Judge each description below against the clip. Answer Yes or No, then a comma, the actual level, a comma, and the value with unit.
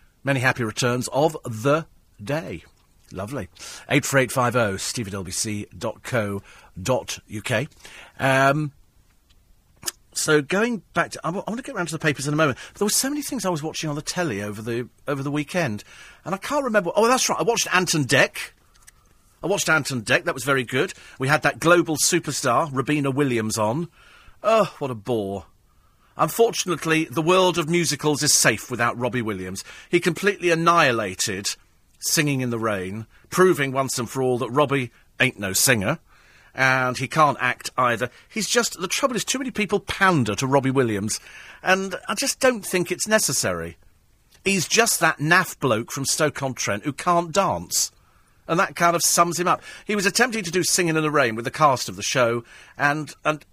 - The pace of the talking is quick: No, average, 175 wpm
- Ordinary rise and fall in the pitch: No, wide, 6.7 semitones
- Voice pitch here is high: No, medium, 145 Hz